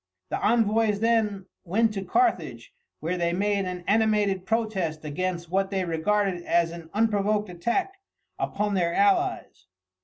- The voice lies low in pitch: No, high, 200 Hz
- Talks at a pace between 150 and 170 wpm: No, average, 140 wpm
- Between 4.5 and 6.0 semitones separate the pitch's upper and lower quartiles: No, average, 3.8 semitones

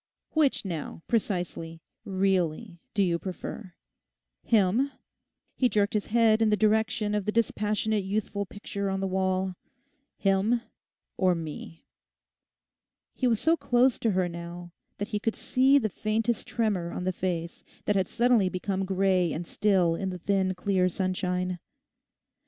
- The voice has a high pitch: Yes, high, 195 Hz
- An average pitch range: Yes, average, 3.1 semitones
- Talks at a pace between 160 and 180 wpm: No, average, 145 wpm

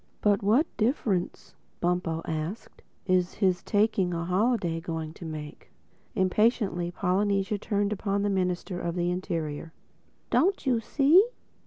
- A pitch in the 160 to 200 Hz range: Yes, medium, 185 Hz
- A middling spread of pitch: Yes, average, 3.4 semitones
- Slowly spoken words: Yes, slow, 130 wpm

